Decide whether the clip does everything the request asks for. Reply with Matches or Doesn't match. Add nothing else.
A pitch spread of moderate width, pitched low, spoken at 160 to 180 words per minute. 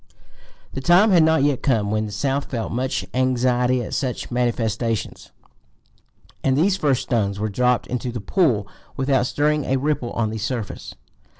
Matches